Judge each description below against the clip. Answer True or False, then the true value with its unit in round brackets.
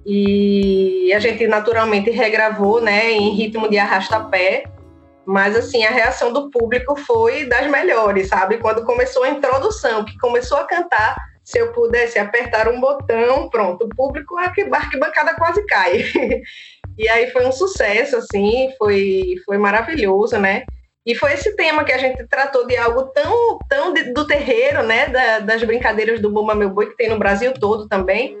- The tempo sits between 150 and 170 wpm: True (165 wpm)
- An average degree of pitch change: False (5.8 semitones)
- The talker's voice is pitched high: True (235 Hz)